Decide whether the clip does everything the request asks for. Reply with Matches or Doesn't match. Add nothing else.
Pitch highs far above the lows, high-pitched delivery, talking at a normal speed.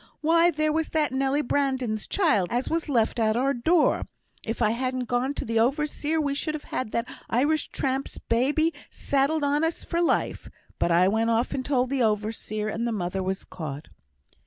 Doesn't match